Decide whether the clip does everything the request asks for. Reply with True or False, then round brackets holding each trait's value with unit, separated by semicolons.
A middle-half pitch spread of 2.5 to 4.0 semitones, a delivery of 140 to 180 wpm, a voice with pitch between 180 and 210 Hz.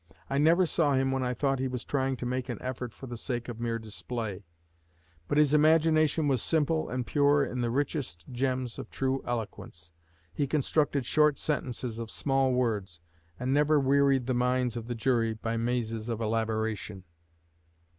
False (3.5 semitones; 175 wpm; 125 Hz)